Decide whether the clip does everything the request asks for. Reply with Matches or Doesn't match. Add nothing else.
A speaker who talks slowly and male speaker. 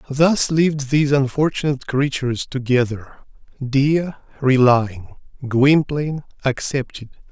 Matches